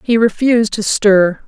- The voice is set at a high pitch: Yes, high, 215 Hz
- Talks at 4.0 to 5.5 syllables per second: Yes, 4.6 syllables/s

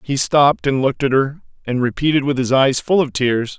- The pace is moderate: No, fast, 235 wpm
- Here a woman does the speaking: No, male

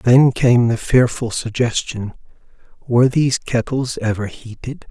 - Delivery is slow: Yes, slow, 120 wpm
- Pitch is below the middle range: Yes, low, 120 Hz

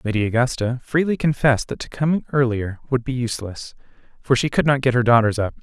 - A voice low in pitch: Yes, low, 125 Hz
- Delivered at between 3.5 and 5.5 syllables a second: No, 6.0 syllables/s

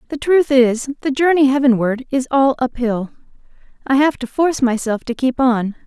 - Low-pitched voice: No, very high, 260 Hz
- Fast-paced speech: No, average, 185 wpm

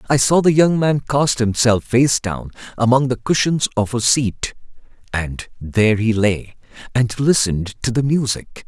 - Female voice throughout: No, male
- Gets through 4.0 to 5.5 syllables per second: Yes, 4.4 syllables/s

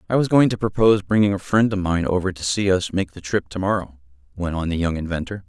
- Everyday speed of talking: No, fast, 265 wpm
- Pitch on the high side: No, very low, 95 Hz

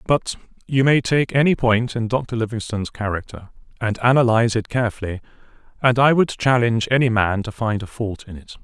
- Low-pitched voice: Yes, low, 115 Hz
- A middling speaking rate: Yes, average, 180 wpm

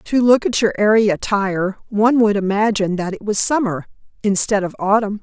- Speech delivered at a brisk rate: No, average, 185 wpm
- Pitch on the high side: Yes, high, 205 Hz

